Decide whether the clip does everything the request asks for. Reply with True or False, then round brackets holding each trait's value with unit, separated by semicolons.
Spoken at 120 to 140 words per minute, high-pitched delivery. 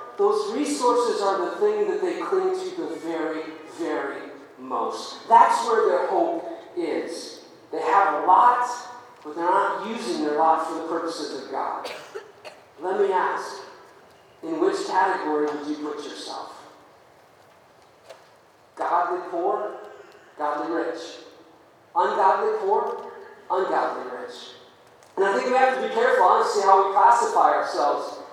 True (135 wpm; 245 Hz)